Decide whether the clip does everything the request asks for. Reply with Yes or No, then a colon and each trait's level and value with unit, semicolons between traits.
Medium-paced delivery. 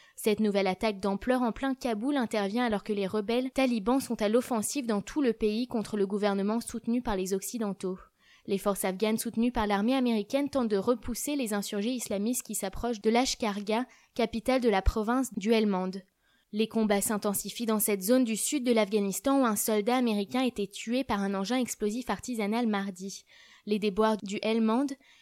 Yes: average, 180 wpm